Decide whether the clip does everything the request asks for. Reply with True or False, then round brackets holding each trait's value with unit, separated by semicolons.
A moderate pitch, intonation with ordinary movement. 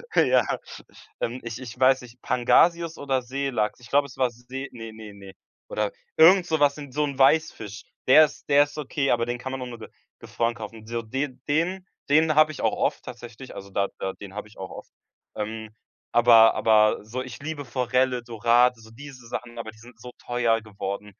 False (125 Hz; 3.8 semitones)